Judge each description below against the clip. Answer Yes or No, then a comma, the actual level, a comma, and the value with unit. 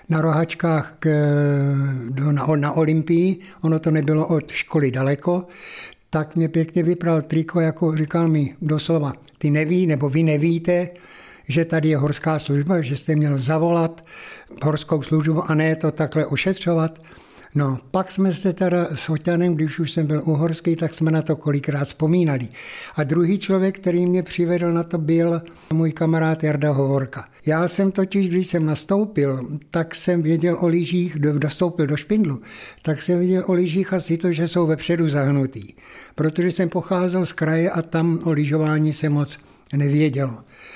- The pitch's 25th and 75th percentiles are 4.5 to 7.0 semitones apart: No, narrow, 2.5 semitones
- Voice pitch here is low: No, medium, 160 Hz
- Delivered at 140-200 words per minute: Yes, average, 160 wpm